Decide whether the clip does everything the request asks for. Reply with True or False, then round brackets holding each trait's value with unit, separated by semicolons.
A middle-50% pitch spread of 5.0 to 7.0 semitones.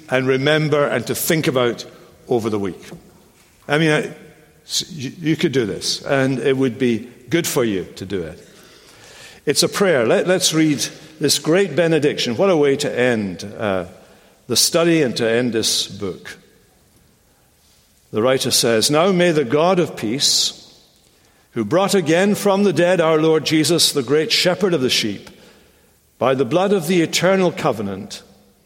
True (5.6 semitones)